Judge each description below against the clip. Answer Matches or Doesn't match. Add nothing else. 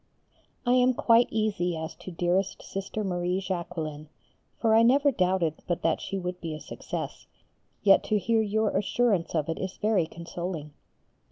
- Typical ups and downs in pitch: Matches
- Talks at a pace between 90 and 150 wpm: Doesn't match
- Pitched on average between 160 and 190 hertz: Matches